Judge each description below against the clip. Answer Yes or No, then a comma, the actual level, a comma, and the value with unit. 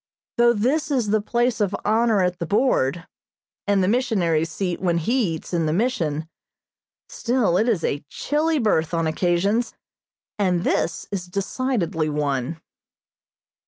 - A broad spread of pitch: Yes, wide, 6.1 semitones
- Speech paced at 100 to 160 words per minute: Yes, average, 145 wpm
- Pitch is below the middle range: No, high, 190 Hz